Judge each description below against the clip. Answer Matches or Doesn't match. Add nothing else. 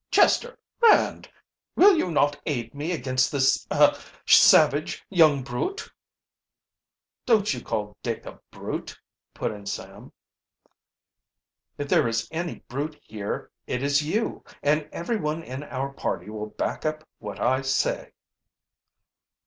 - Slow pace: Matches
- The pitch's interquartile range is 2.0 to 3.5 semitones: Doesn't match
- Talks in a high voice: Doesn't match